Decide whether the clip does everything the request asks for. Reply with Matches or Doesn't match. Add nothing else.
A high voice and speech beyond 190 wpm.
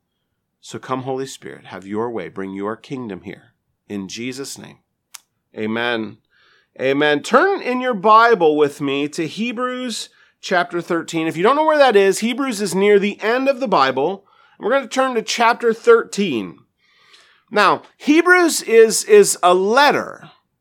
Doesn't match